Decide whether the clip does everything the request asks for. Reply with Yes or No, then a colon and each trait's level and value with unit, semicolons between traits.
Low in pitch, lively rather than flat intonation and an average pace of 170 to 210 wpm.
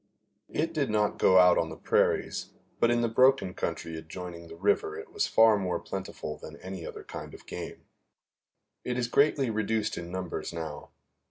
Yes: low, 100 Hz; wide, 5.9 semitones; average, 180 wpm